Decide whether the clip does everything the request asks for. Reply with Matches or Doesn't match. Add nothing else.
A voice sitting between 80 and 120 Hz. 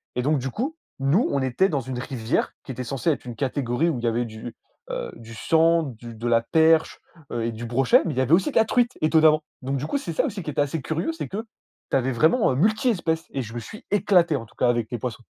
Doesn't match